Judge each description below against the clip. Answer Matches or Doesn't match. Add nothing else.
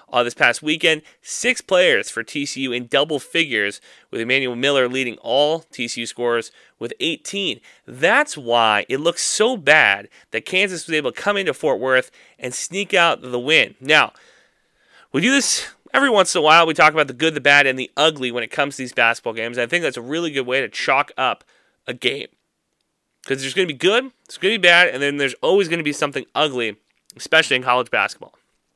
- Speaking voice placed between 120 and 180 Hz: Matches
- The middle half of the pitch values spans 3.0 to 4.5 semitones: Doesn't match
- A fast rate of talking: Matches